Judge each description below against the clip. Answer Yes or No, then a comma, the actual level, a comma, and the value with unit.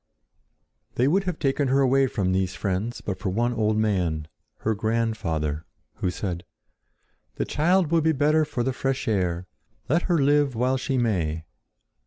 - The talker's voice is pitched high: No, low, 115 Hz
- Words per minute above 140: Yes, average, 165 wpm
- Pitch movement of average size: No, wide, 6.8 semitones